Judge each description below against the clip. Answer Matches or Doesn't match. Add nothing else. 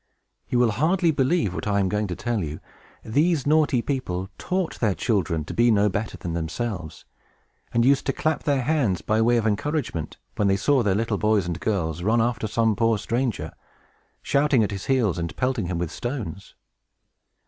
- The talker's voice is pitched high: Doesn't match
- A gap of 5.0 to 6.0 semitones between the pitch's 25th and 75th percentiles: Matches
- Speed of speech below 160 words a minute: Doesn't match